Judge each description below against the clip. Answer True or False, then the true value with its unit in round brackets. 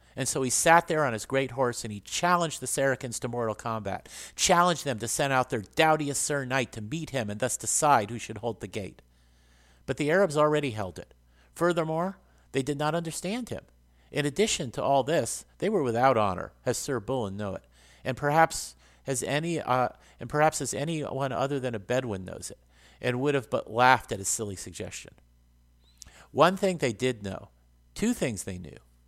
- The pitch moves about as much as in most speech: False (7.1 semitones)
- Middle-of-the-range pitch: False (125 Hz)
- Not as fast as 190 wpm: False (200 wpm)